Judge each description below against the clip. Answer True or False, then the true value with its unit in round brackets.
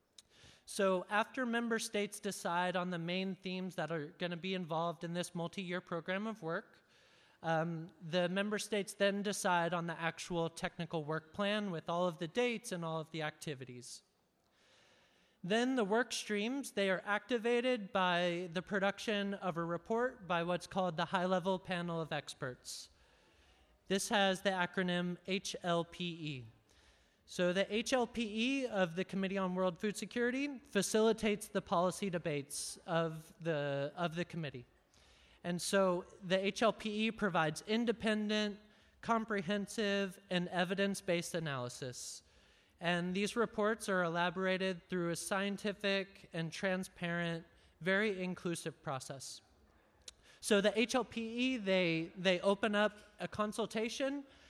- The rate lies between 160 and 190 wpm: False (135 wpm)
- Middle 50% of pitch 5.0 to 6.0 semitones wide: False (3.5 semitones)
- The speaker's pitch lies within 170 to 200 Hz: True (185 Hz)